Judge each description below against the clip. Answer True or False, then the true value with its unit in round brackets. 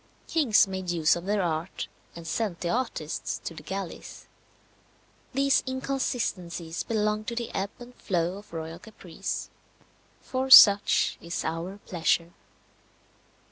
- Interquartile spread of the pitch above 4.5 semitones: True (5.2 semitones)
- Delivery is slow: True (130 wpm)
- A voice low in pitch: False (190 Hz)